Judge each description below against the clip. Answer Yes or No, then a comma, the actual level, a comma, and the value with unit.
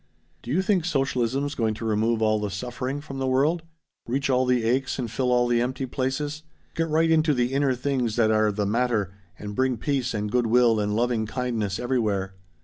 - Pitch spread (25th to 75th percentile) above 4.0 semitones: No, average, 3.5 semitones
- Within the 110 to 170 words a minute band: No, fast, 205 wpm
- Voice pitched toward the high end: No, low, 125 Hz